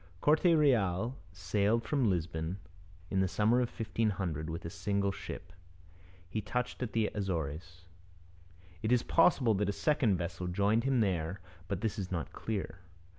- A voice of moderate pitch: No, low, 100 Hz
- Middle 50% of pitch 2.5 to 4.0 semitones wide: No, average, 4.4 semitones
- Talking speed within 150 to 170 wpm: Yes, average, 155 wpm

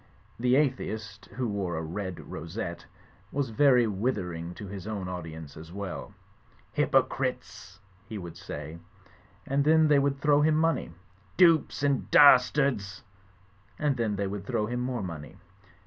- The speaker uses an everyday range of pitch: No, wide, 7.2 semitones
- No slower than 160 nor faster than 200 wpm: No, average, 150 wpm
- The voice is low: Yes, low, 105 Hz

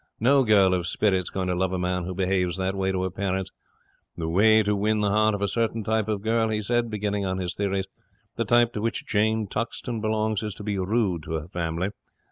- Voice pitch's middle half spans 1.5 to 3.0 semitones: Yes, average, 2.7 semitones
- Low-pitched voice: Yes, low, 100 Hz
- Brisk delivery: Yes, fast, 235 wpm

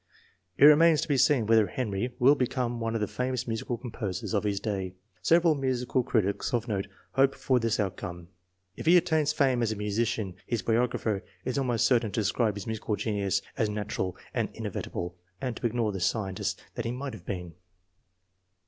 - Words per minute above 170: Yes, average, 190 wpm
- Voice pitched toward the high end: No, low, 115 Hz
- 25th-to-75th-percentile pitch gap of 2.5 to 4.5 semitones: Yes, average, 3.8 semitones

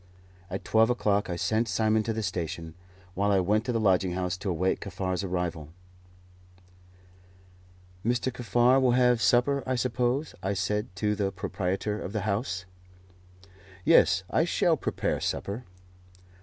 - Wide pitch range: No, average, 4.3 semitones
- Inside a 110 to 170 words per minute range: Yes, average, 145 wpm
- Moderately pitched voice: No, low, 105 Hz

